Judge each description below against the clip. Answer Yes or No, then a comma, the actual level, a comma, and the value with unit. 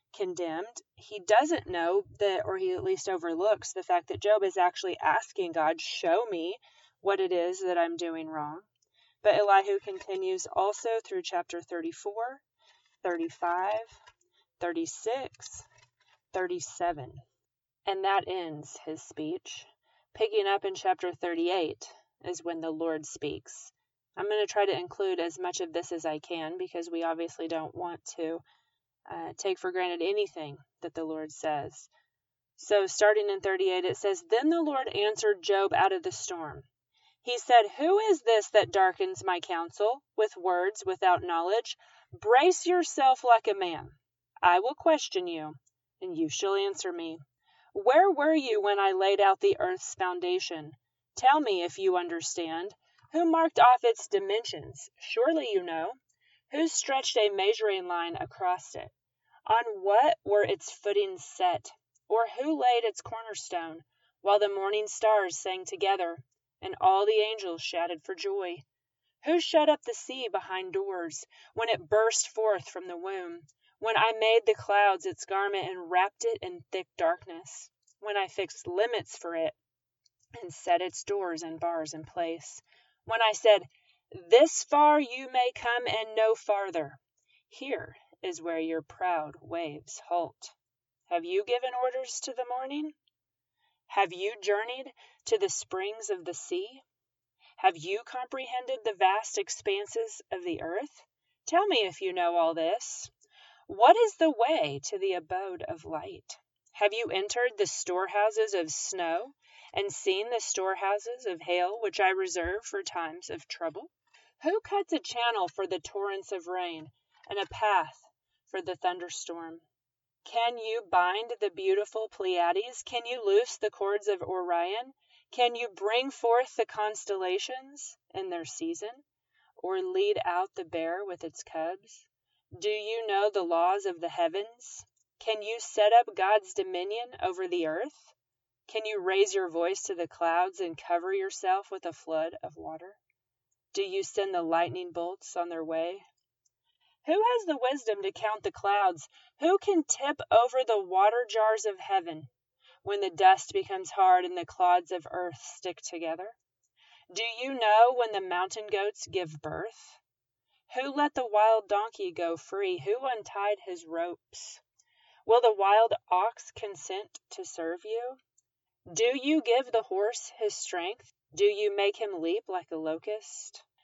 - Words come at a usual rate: Yes, average, 160 wpm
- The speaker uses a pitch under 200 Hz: No, high, 210 Hz